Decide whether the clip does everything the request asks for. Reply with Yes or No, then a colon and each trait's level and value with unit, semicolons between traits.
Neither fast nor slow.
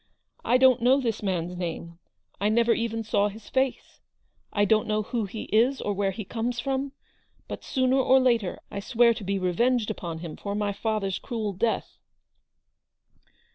Yes: average, 175 wpm